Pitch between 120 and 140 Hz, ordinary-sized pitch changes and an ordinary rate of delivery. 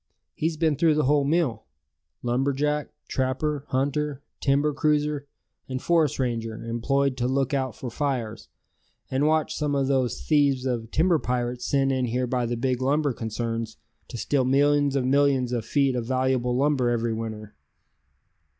Yes: low, 135 Hz; average, 3.0 semitones; average, 160 wpm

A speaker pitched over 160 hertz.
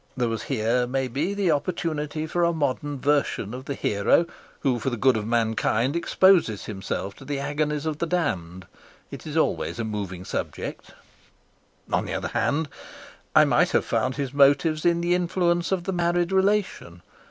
No: medium, 145 Hz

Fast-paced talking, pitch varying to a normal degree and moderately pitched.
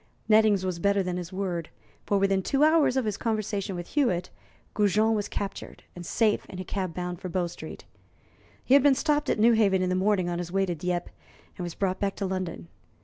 No: fast, 215 wpm; average, 3.1 semitones; high, 195 Hz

